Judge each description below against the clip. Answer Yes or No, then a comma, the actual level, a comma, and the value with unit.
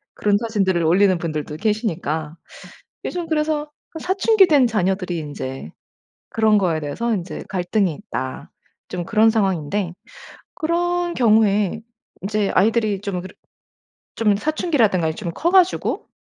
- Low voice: No, high, 205 Hz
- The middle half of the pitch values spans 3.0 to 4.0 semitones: No, average, 5.1 semitones